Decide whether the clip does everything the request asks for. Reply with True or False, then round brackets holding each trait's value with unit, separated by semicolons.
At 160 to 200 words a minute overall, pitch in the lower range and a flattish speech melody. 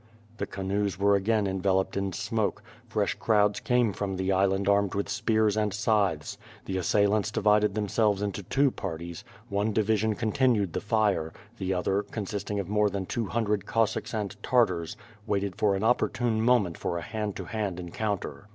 True (170 wpm; 100 Hz; 2.0 semitones)